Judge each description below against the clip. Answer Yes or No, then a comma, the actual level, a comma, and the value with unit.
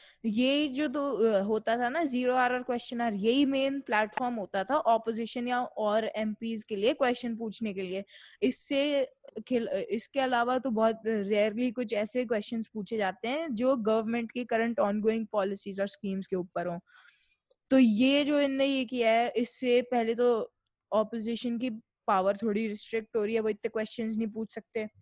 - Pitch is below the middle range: No, high, 230 Hz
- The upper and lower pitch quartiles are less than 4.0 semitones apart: Yes, narrow, 2.6 semitones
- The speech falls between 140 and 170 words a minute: No, average, 180 wpm